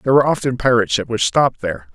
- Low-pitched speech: Yes, low, 120 Hz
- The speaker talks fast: Yes, fast, 245 wpm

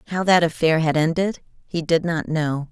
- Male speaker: No, female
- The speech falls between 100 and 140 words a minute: No, average, 200 wpm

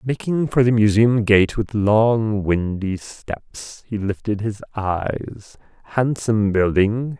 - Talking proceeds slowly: Yes, slow, 125 wpm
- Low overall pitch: Yes, low, 110 Hz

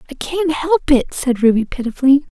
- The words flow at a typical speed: Yes, average, 180 wpm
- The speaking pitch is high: Yes, very high, 280 Hz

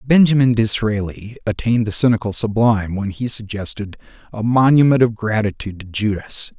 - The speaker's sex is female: No, male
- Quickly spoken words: No, slow, 135 wpm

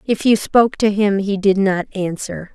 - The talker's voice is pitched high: Yes, high, 200 Hz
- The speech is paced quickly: Yes, fast, 210 wpm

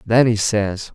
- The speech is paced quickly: No, average, 190 wpm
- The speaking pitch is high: No, low, 110 Hz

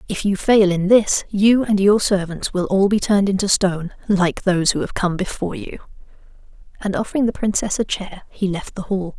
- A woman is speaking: Yes, female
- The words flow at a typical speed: No, fast, 210 wpm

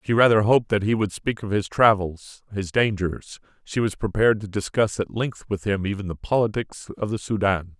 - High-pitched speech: No, low, 105 Hz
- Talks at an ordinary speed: No, fast, 210 wpm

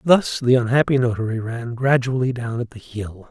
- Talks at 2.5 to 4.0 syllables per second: No, 5.0 syllables/s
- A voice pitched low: Yes, low, 120 Hz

